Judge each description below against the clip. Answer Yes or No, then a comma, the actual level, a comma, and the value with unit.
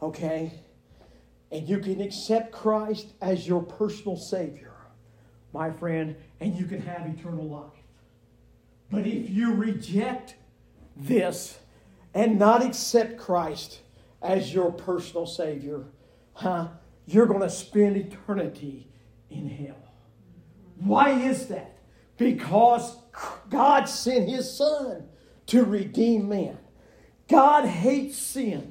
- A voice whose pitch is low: No, high, 190 Hz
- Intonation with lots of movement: Yes, wide, 6.6 semitones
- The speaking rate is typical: No, slow, 110 wpm